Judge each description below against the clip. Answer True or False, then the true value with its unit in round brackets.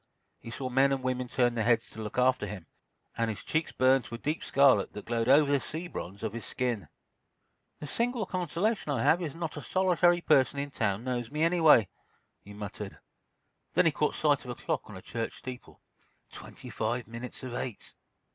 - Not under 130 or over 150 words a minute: False (205 wpm)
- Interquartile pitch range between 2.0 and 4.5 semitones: False (4.9 semitones)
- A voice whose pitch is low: True (130 Hz)